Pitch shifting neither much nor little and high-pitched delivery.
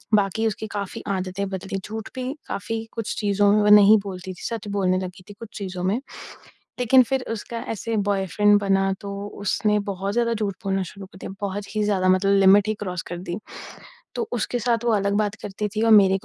No: narrow, 2.0 semitones; high, 200 Hz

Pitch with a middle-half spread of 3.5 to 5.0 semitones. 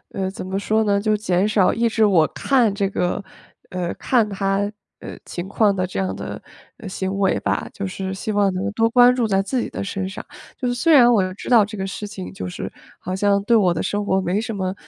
No: narrow, 2.6 semitones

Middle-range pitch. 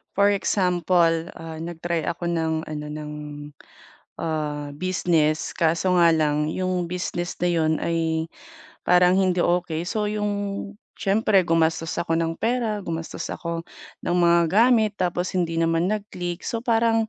Yes: medium, 175 Hz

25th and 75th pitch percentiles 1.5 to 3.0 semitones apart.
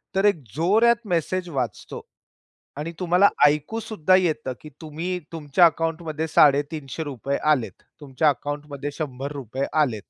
No: average, 3.7 semitones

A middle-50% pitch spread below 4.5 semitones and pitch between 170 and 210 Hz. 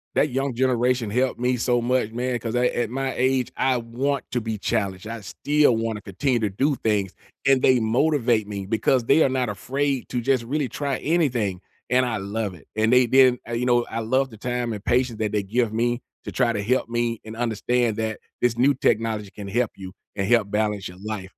No: average, 2.8 semitones; low, 120 Hz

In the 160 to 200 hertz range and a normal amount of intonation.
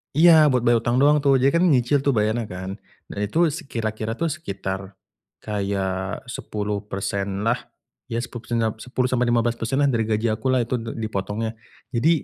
No: low, 115 Hz; average, 3.4 semitones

